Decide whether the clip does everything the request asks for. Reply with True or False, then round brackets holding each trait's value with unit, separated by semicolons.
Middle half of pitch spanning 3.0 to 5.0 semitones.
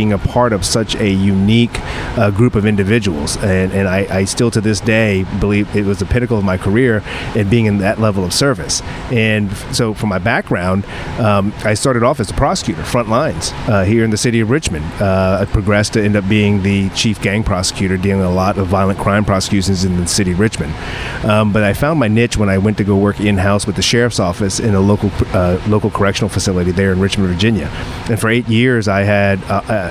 False (2.5 semitones)